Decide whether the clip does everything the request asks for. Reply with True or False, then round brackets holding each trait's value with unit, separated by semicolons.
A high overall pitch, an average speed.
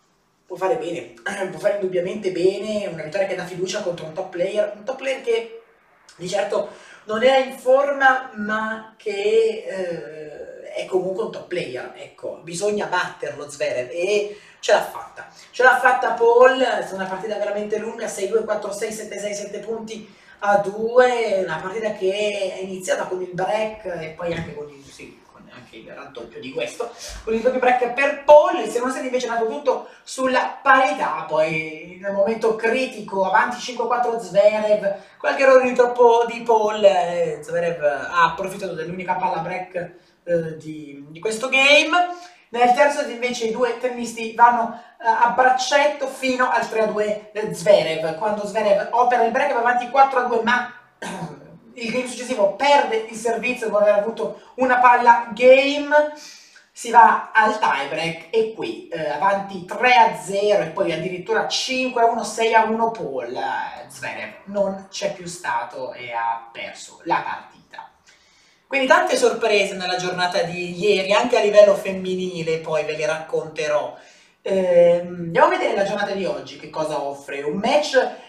True (210 Hz; 160 wpm)